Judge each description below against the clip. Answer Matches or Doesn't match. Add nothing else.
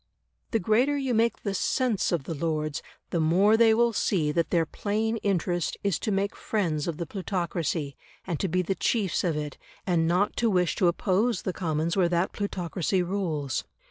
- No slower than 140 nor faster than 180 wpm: Doesn't match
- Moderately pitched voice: Matches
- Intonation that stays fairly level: Doesn't match